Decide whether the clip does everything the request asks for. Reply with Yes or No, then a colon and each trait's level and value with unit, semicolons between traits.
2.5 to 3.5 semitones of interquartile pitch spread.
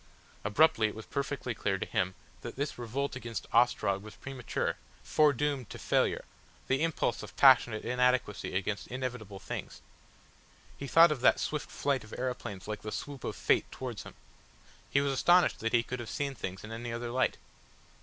No: average, 4.2 semitones